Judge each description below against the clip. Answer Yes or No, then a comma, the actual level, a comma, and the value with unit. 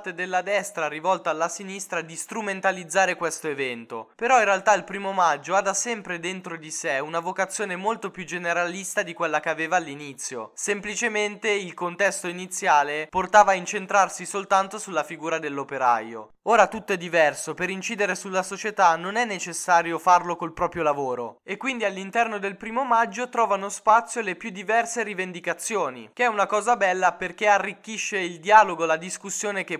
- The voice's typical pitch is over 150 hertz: Yes, high, 190 Hz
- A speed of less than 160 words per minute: No, average, 165 wpm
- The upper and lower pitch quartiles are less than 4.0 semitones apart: Yes, average, 3.3 semitones